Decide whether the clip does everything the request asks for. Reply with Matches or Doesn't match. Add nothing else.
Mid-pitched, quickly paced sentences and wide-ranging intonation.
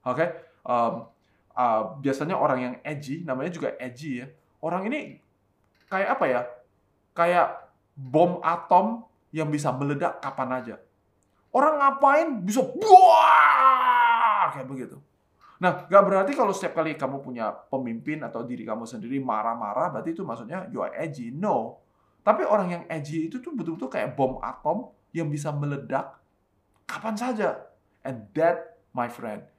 Matches